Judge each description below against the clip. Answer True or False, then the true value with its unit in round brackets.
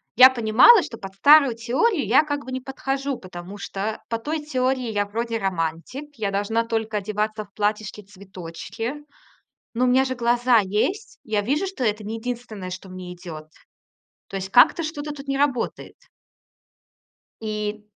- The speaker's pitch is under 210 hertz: False (225 Hz)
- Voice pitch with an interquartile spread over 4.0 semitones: True (4.5 semitones)